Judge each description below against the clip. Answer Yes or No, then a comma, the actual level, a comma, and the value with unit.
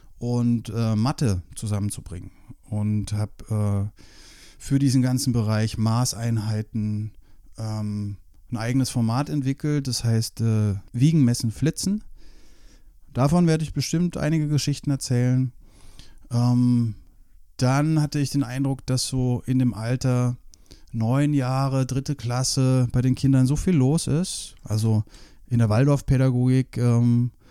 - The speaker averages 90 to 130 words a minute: Yes, slow, 125 wpm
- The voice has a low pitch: Yes, low, 125 Hz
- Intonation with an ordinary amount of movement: Yes, average, 3.8 semitones